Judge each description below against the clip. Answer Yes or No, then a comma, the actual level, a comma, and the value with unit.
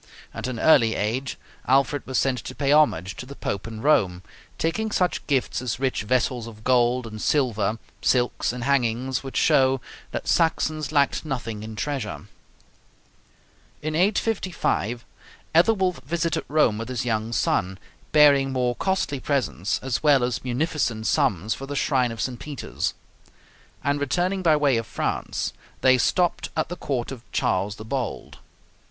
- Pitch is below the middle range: Yes, low, 130 Hz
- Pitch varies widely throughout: No, average, 4.5 semitones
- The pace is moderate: Yes, average, 155 wpm